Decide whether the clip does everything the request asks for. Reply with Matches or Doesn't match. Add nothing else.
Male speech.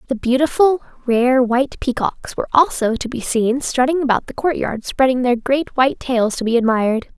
Doesn't match